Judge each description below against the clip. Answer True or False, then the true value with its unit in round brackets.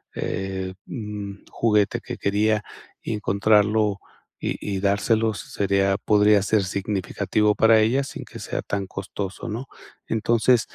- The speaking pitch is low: True (105 Hz)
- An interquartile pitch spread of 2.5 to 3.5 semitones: False (1.8 semitones)